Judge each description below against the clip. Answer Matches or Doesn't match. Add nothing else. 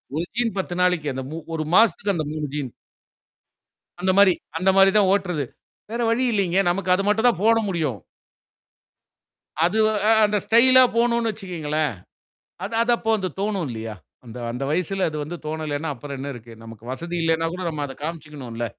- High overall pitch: Doesn't match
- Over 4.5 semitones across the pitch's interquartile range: Matches